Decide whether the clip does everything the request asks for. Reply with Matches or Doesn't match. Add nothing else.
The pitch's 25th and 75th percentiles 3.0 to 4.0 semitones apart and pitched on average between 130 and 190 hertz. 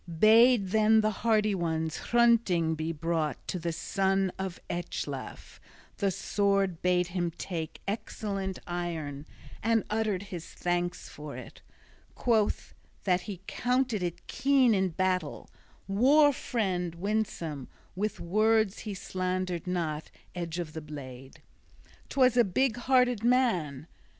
Doesn't match